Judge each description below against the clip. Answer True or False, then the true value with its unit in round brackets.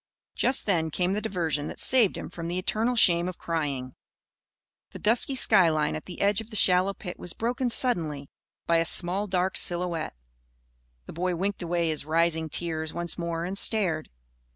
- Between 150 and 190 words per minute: True (175 wpm)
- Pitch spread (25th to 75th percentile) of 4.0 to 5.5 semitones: False (3.5 semitones)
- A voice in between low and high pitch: True (175 Hz)